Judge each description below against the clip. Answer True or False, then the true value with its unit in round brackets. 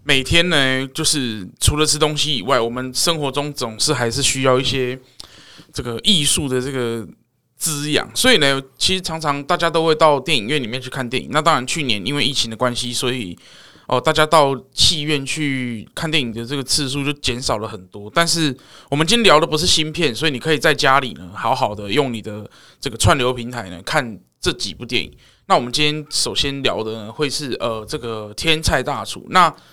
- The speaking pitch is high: False (135 Hz)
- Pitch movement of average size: True (3.8 semitones)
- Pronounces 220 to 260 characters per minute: False (305 characters per minute)